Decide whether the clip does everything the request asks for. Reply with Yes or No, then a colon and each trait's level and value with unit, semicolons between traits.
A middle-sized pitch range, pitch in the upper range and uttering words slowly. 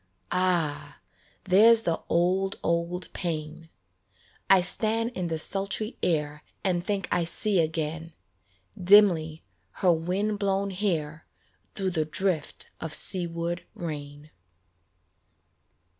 No: average, 3.2 semitones; medium, 175 Hz; slow, 105 wpm